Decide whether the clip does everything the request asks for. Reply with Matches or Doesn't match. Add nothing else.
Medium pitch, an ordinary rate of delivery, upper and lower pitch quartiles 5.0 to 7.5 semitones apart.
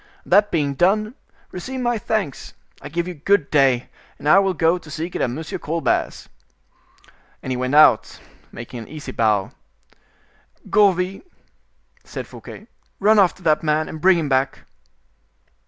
Matches